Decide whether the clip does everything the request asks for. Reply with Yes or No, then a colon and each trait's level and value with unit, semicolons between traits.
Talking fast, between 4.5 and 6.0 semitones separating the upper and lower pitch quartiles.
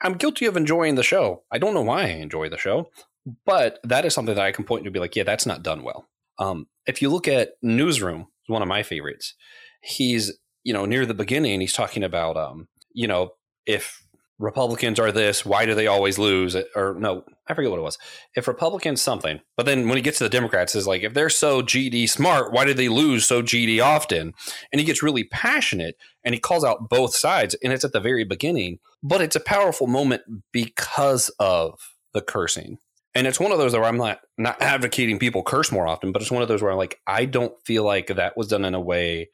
Yes: fast, 230 wpm; wide, 5.5 semitones